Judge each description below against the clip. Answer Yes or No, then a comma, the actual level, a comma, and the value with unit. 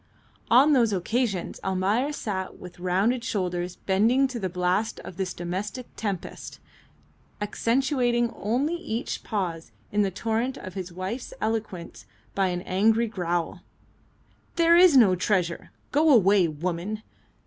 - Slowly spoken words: Yes, slow, 130 wpm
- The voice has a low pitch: No, high, 205 Hz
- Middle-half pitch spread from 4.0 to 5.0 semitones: Yes, average, 4.7 semitones